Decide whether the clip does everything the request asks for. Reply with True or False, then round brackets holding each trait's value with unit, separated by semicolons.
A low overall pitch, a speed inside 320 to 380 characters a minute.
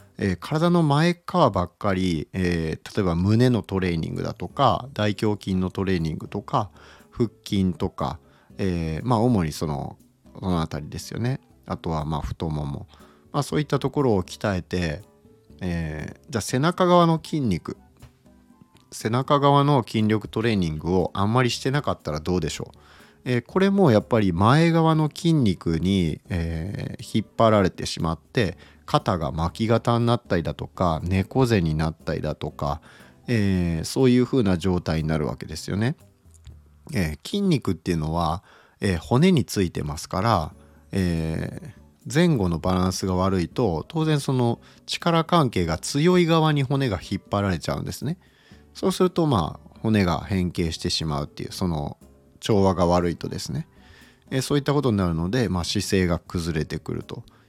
True (95 Hz; 325 characters per minute)